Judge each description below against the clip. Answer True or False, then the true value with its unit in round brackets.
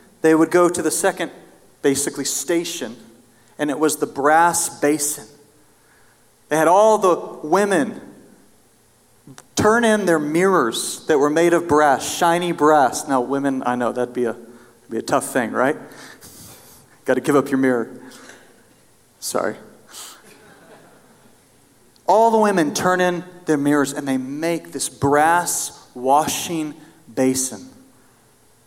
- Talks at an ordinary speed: False (130 wpm)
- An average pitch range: True (4.3 semitones)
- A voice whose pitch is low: False (150 Hz)